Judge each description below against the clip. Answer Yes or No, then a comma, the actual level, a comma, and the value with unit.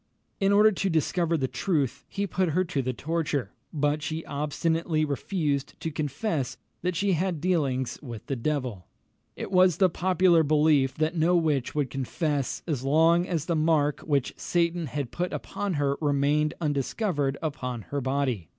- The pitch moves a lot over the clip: No, average, 3.4 semitones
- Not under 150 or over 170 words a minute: Yes, average, 165 wpm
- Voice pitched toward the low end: No, medium, 155 Hz